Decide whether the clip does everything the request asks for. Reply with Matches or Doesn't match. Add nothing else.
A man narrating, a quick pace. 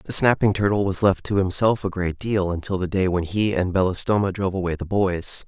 Matches